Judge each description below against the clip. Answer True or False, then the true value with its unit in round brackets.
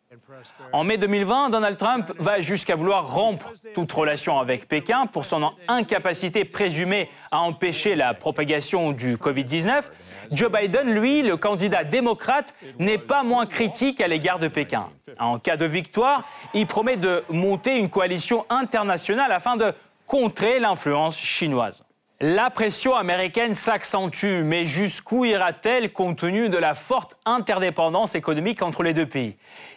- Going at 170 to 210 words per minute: False (145 wpm)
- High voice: True (195 Hz)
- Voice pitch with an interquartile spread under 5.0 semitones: False (5.4 semitones)